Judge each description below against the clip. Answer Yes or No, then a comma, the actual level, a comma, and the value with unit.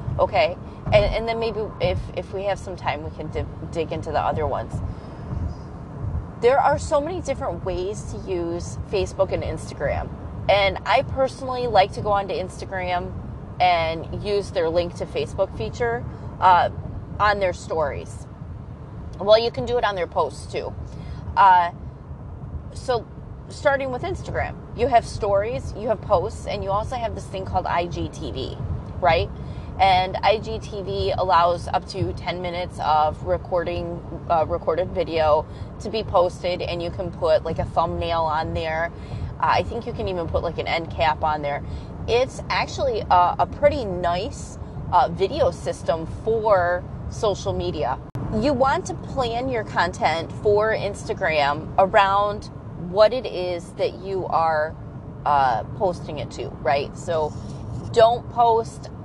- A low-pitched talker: No, high, 190 Hz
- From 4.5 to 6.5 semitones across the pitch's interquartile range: Yes, average, 5.3 semitones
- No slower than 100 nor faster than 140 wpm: No, average, 150 wpm